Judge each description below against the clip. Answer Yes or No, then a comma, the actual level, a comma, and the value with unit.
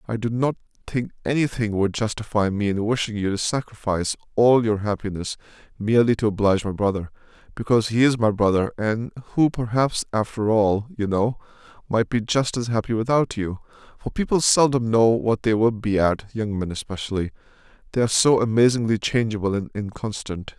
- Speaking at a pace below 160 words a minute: No, average, 170 wpm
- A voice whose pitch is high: No, low, 110 Hz